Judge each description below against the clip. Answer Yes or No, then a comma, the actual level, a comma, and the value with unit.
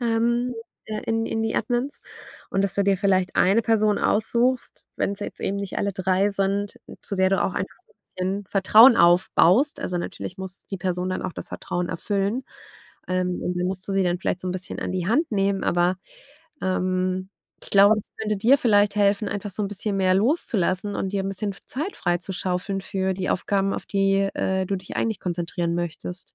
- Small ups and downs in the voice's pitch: Yes, narrow, 2.1 semitones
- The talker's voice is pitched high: Yes, high, 195 Hz